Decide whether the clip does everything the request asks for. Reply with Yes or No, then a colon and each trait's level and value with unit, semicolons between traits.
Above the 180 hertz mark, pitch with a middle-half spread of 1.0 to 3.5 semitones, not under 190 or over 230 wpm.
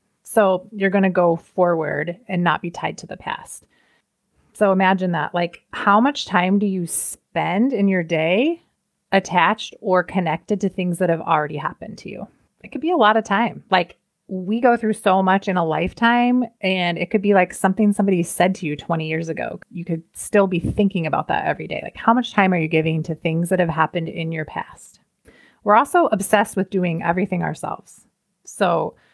Yes: high, 190 Hz; average, 3.2 semitones; average, 200 wpm